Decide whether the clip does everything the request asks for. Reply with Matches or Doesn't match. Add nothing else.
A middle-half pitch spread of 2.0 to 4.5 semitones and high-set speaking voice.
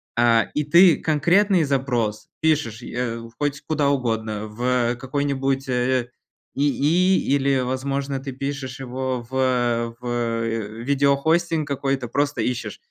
Doesn't match